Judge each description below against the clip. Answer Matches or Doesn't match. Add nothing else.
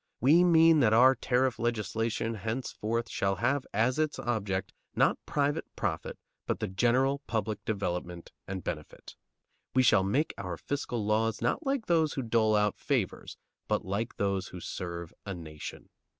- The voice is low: Matches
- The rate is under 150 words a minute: Doesn't match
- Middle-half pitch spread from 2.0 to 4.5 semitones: Doesn't match